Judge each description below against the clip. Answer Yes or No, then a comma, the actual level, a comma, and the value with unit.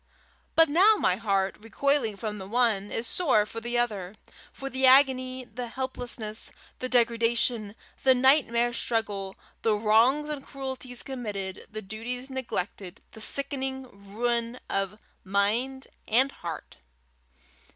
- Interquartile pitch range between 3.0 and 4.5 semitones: Yes, average, 3.7 semitones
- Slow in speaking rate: Yes, slow, 130 wpm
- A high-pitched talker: Yes, high, 235 Hz